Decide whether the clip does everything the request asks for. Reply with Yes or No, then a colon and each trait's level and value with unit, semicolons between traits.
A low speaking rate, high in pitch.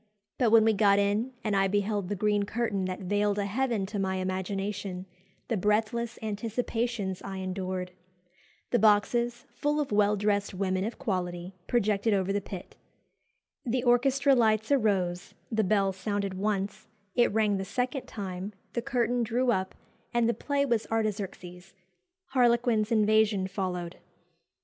No: average, 150 wpm; high, 205 Hz